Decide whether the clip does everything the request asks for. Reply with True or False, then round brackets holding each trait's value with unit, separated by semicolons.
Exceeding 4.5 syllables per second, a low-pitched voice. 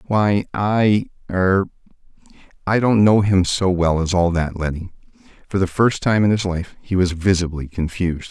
True (4.7 syllables/s; 95 Hz)